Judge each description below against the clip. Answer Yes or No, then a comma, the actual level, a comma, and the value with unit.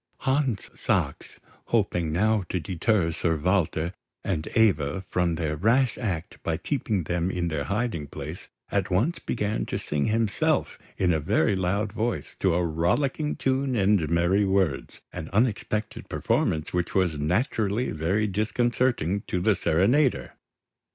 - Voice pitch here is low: Yes, very low, 95 Hz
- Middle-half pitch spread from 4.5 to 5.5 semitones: Yes, average, 5.0 semitones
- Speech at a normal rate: Yes, average, 145 wpm